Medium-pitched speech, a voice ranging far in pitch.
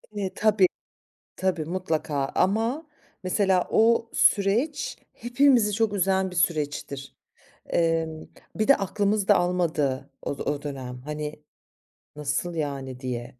Yes: medium, 180 Hz; wide, 5.8 semitones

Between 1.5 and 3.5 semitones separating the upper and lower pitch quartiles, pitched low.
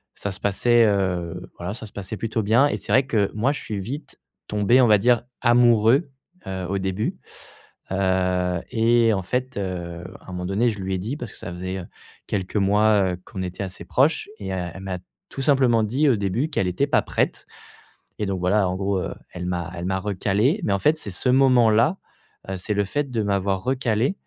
No: average, 4.3 semitones; low, 105 Hz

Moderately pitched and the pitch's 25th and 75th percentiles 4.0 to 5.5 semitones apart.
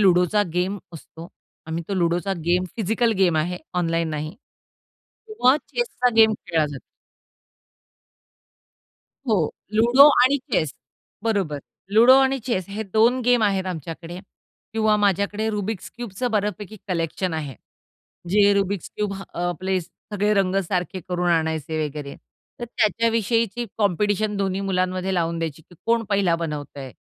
No: high, 195 Hz; average, 4.4 semitones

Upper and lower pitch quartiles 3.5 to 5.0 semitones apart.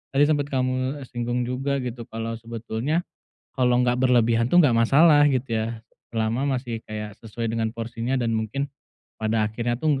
No: narrow, 2.6 semitones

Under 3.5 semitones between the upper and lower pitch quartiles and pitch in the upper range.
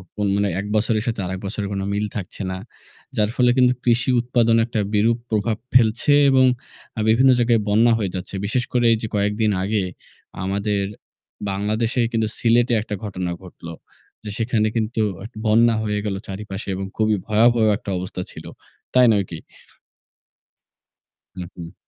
No: narrow, 2.6 semitones; low, 110 Hz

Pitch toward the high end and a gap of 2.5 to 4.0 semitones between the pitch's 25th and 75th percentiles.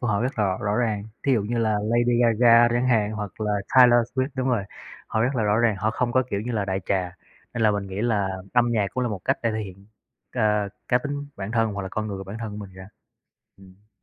No: low, 110 Hz; average, 3.0 semitones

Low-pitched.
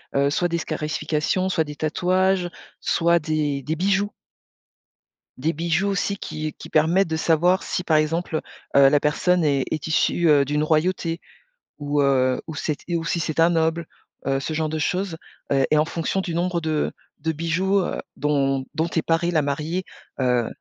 No: medium, 160 Hz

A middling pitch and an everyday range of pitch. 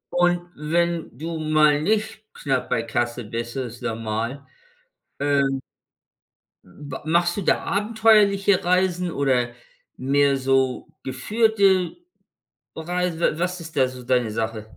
No: medium, 150 Hz; wide, 5.8 semitones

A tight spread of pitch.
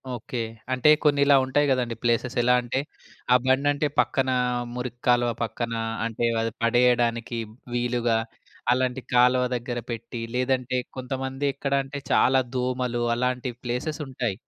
Yes: narrow, 1.7 semitones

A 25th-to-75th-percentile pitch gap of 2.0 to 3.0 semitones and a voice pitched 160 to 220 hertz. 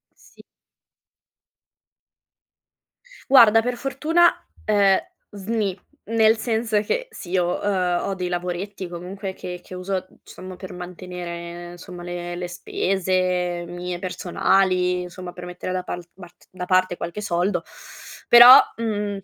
Yes: narrow, 2.5 semitones; medium, 185 Hz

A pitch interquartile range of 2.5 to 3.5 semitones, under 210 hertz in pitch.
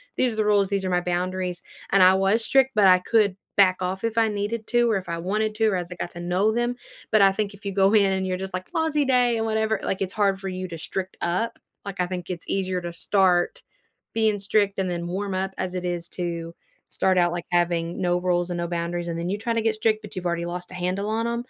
Yes: average, 3.2 semitones; high, 190 Hz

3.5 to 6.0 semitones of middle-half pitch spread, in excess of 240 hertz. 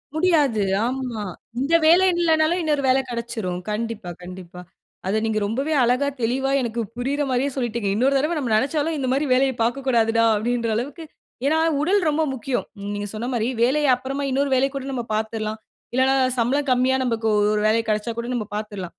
Yes: average, 3.9 semitones; very high, 250 Hz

